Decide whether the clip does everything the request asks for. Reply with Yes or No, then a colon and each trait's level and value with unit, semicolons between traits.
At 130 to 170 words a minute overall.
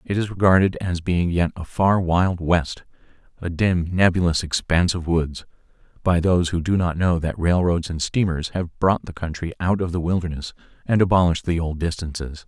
No: average, 180 wpm